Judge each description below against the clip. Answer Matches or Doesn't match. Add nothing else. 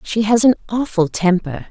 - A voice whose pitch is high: Matches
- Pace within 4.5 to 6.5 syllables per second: Matches